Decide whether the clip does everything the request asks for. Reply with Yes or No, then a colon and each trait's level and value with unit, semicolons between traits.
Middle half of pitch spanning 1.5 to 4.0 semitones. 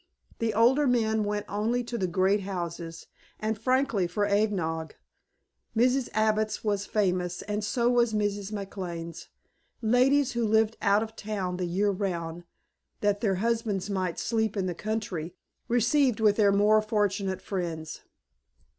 Yes: average, 3.0 semitones